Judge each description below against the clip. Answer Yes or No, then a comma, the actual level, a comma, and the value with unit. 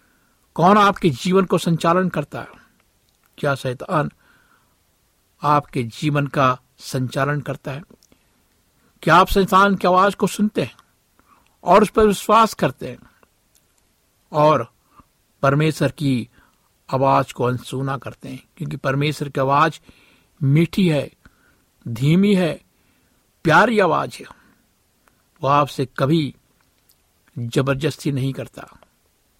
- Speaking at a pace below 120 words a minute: Yes, slow, 110 wpm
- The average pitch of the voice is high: No, medium, 145 Hz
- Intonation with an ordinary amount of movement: Yes, average, 4.9 semitones